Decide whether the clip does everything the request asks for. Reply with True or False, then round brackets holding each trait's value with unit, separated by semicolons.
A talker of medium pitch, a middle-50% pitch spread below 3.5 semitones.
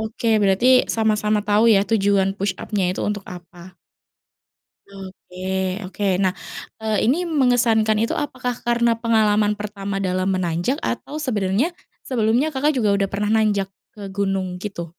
False (210 Hz; 3.0 semitones)